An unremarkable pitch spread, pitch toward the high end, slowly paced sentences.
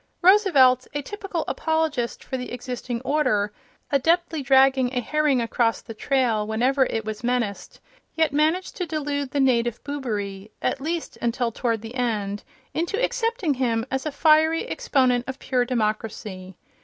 No: average, 4.8 semitones; very high, 260 Hz; average, 155 wpm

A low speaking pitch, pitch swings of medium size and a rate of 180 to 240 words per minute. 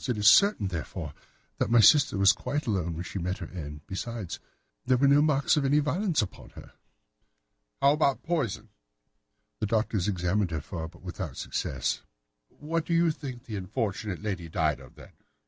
No: low, 105 Hz; wide, 7.8 semitones; average, 185 wpm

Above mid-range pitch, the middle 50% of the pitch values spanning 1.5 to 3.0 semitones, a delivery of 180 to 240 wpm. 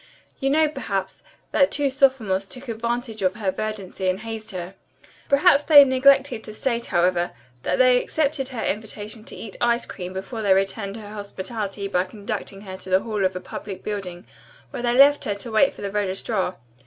No: high, 215 Hz; average, 4.6 semitones; average, 190 wpm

